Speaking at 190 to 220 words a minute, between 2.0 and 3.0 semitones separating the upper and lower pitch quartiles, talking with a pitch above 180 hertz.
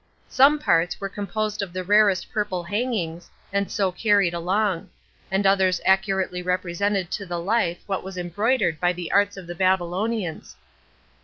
No: average, 155 wpm; narrow, 2.6 semitones; high, 190 Hz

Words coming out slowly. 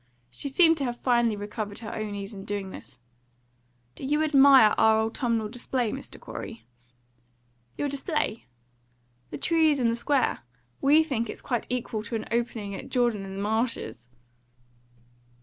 No: average, 150 wpm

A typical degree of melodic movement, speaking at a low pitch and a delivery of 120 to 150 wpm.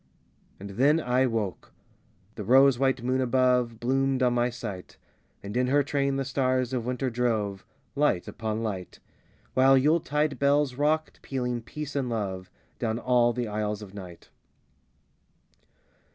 Yes: average, 3.4 semitones; low, 125 Hz; average, 145 wpm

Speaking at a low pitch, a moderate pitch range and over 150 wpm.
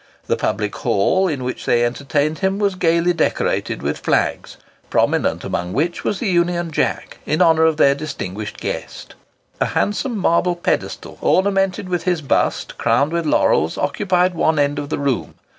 No: medium, 165 Hz; average, 4.4 semitones; average, 165 wpm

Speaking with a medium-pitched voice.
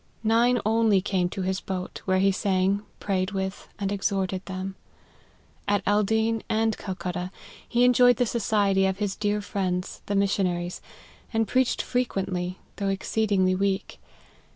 No: high, 195 Hz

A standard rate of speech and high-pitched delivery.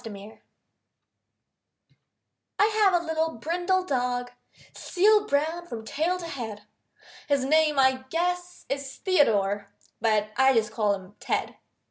No: slow, 125 wpm; very high, 275 Hz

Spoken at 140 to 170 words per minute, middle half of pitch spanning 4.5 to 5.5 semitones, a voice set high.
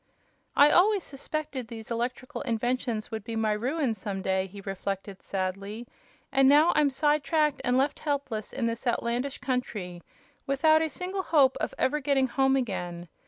Yes: average, 165 wpm; average, 4.9 semitones; very high, 250 Hz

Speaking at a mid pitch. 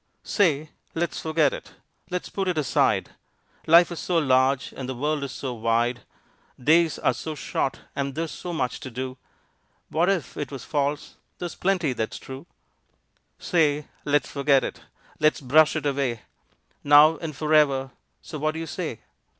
Yes: medium, 150 Hz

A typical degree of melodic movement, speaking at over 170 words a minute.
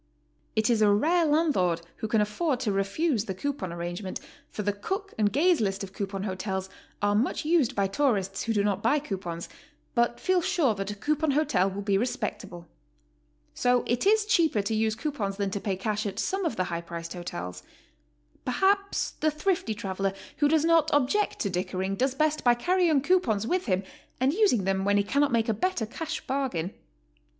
No: wide, 7.6 semitones; average, 195 wpm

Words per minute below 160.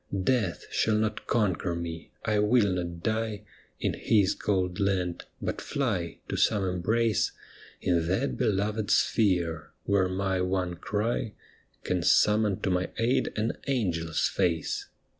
Yes: slow, 135 wpm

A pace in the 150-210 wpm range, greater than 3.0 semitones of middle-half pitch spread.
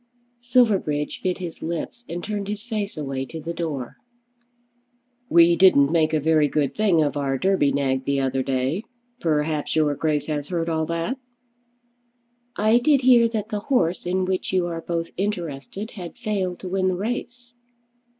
Yes: average, 170 wpm; wide, 5.4 semitones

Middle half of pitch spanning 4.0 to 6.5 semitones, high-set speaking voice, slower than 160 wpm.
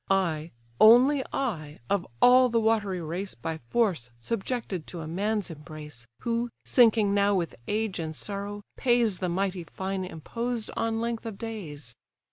Yes: average, 5.3 semitones; high, 200 Hz; average, 150 wpm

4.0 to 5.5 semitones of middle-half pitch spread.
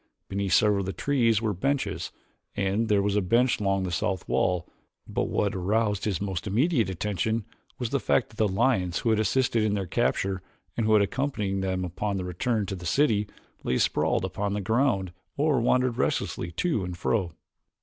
No: average, 3.3 semitones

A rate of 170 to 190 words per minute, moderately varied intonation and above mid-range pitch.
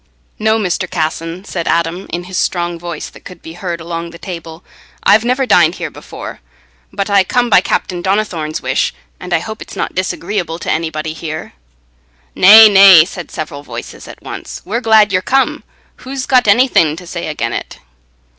No: average, 180 wpm; average, 3.9 semitones; medium, 180 Hz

